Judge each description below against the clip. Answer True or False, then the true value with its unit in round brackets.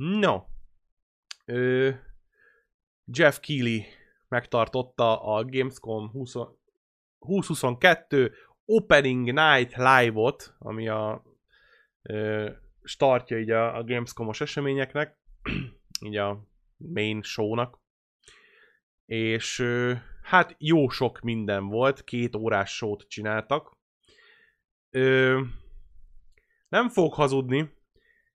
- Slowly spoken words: True (85 wpm)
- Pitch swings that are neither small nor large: True (4.7 semitones)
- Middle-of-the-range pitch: False (125 Hz)